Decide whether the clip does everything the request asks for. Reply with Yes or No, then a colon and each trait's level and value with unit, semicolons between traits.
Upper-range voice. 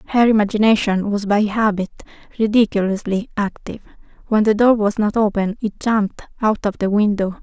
Yes: high, 210 Hz